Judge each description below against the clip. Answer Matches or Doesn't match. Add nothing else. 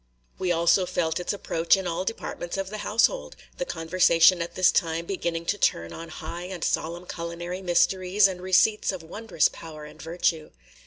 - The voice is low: Doesn't match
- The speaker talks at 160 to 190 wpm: Matches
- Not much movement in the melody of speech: Matches